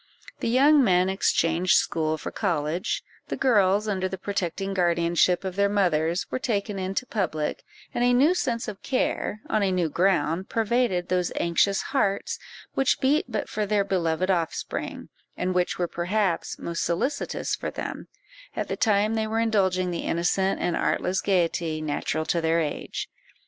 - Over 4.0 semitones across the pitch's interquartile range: No, average, 3.7 semitones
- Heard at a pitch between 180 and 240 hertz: Yes, high, 190 Hz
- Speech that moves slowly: No, average, 165 wpm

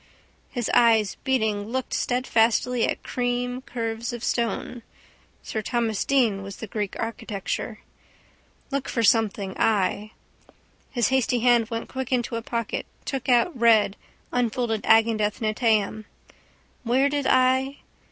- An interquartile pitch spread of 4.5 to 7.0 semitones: No, narrow, 2.4 semitones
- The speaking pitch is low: No, high, 230 Hz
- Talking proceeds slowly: Yes, slow, 125 wpm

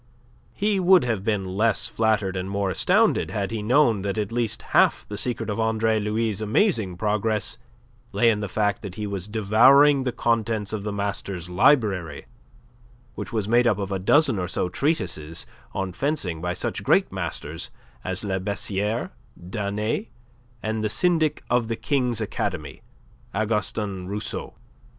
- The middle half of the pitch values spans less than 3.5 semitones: Yes, average, 3.0 semitones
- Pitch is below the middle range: Yes, low, 105 Hz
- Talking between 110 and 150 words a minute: No, average, 160 wpm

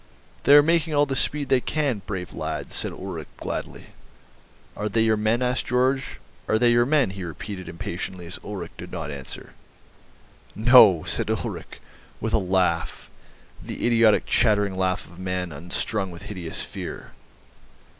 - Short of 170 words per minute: Yes, average, 160 wpm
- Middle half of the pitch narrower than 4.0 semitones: No, wide, 5.6 semitones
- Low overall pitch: Yes, low, 105 Hz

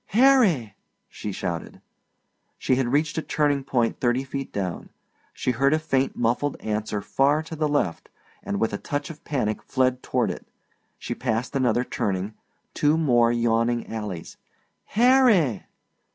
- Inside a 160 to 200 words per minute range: No, average, 150 wpm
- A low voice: Yes, low, 130 Hz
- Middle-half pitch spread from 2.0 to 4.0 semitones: No, average, 4.7 semitones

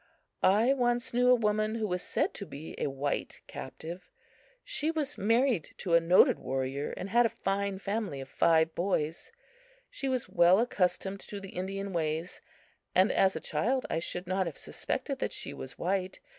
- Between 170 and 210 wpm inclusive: Yes, average, 180 wpm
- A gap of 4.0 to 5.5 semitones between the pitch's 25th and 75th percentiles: Yes, average, 5.1 semitones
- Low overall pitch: No, high, 190 Hz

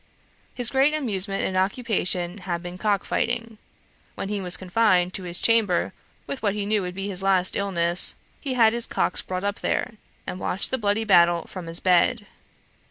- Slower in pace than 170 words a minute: No, average, 185 wpm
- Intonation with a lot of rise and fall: No, average, 3.7 semitones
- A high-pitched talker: Yes, high, 195 Hz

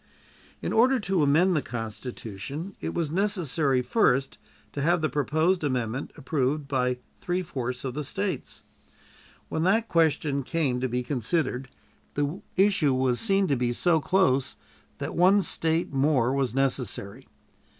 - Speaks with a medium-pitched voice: Yes, medium, 145 Hz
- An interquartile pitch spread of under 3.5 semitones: No, wide, 5.4 semitones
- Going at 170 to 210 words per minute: No, average, 150 wpm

